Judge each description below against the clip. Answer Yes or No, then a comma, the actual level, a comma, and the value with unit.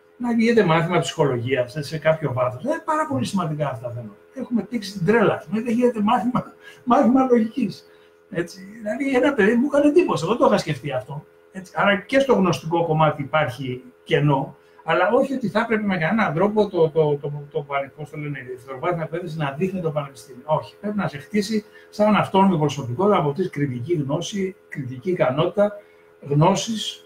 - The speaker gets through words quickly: Yes, fast, 175 wpm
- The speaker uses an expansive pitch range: Yes, wide, 6.7 semitones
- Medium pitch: Yes, medium, 170 Hz